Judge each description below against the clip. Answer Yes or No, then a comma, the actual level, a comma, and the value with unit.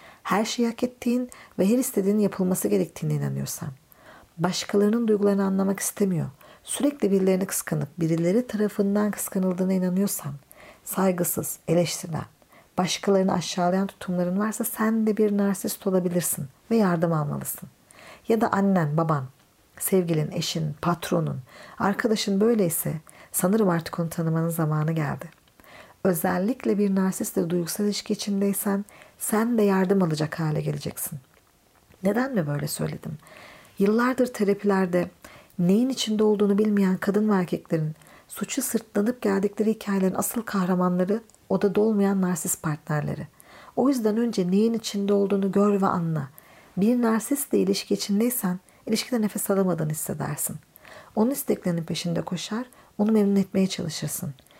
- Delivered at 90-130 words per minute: Yes, average, 120 wpm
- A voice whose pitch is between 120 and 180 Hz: No, high, 195 Hz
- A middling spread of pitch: Yes, average, 3.4 semitones